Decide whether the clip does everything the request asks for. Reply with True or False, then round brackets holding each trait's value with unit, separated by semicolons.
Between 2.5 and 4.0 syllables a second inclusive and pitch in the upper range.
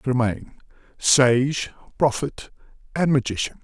False (3.9 syllables/s; 130 Hz)